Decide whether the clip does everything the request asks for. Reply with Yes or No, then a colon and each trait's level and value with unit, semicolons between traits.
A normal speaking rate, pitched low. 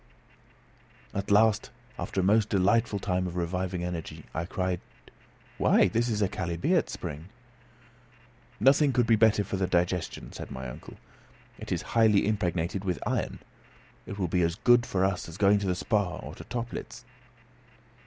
Yes: average, 165 wpm; very low, 95 Hz